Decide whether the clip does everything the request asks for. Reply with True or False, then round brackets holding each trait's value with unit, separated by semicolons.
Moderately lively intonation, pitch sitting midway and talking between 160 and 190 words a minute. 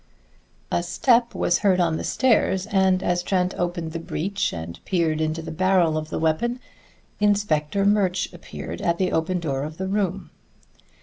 True (3.4 semitones; 175 Hz; 170 wpm)